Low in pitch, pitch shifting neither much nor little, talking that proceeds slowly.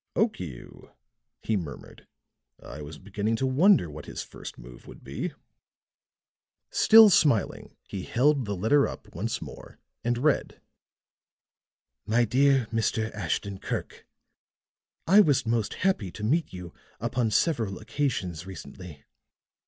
No: low, 110 Hz; wide, 6.9 semitones; slow, 125 wpm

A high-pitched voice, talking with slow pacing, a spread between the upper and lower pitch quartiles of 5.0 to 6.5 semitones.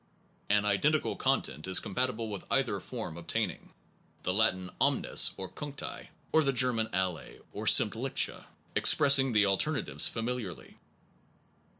No: low, 110 Hz; slow, 125 wpm; wide, 5.5 semitones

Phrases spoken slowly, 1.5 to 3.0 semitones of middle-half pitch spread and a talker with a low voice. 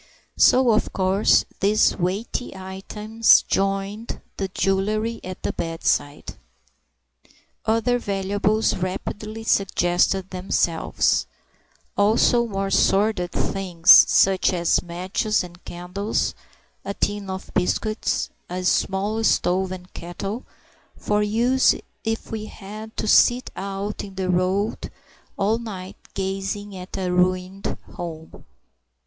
No: slow, 110 wpm; narrow, 2.6 semitones; high, 195 Hz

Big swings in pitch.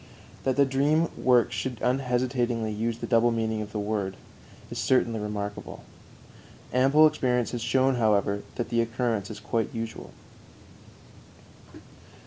No: average, 2.9 semitones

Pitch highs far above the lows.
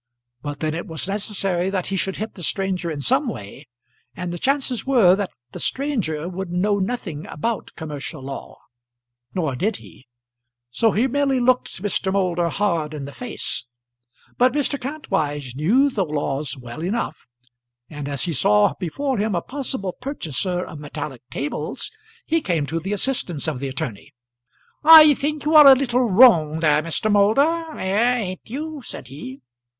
Yes: wide, 8.4 semitones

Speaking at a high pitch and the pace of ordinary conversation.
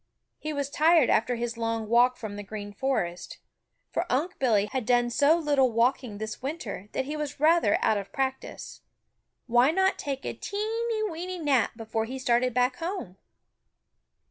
Yes: very high, 255 Hz; average, 170 wpm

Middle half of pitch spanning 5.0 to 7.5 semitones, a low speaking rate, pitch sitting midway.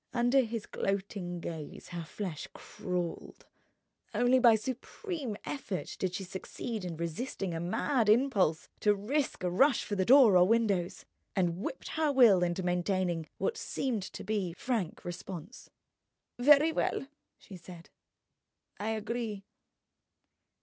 No: wide, 5.4 semitones; slow, 130 wpm; high, 200 Hz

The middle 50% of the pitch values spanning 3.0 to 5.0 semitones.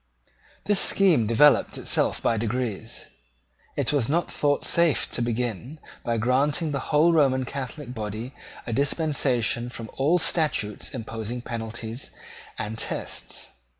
Yes: average, 4.5 semitones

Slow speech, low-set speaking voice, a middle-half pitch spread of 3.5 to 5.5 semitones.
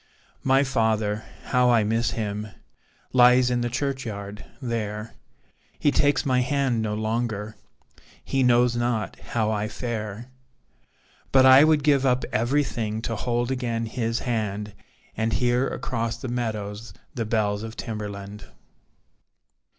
No: slow, 130 wpm; low, 115 Hz; average, 2.7 semitones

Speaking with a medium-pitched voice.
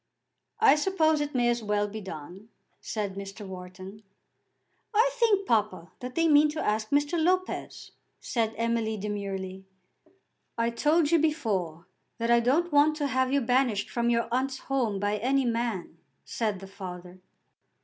No: high, 230 Hz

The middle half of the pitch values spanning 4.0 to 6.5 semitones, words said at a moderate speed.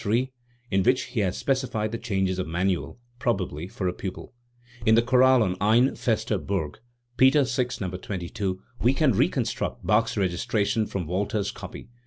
Yes: average, 4.4 semitones; average, 165 wpm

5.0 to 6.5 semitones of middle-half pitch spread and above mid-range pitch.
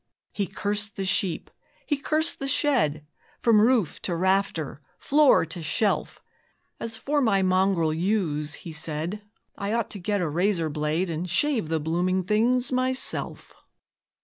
Yes: wide, 5.5 semitones; high, 195 Hz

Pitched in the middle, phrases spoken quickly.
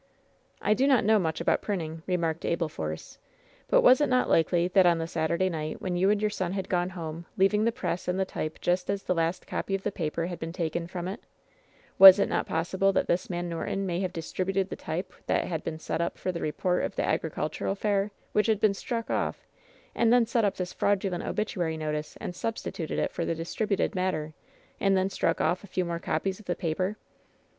Yes: medium, 180 Hz; fast, 225 wpm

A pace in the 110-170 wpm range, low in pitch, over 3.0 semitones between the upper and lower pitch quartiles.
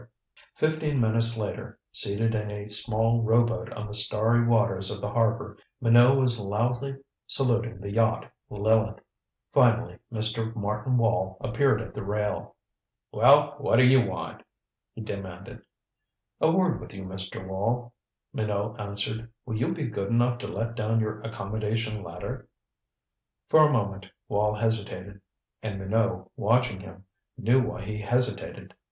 No: average, 140 wpm; low, 110 Hz; narrow, 2.4 semitones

